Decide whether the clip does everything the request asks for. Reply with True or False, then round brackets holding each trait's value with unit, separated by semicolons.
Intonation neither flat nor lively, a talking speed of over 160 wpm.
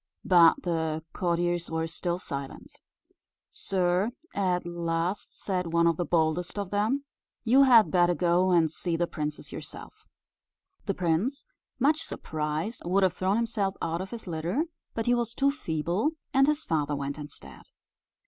False (4.0 semitones; 155 wpm)